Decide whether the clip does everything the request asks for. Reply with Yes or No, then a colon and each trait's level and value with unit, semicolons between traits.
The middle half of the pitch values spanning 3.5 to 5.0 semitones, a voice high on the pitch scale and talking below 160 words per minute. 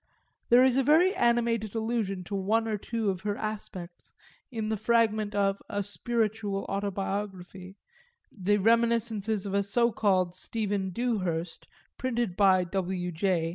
No: average, 3.1 semitones; high, 205 Hz; average, 140 wpm